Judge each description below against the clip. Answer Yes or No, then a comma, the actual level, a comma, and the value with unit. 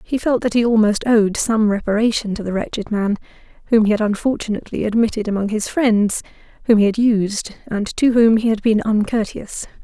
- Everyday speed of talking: Yes, average, 185 wpm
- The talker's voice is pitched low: No, high, 215 Hz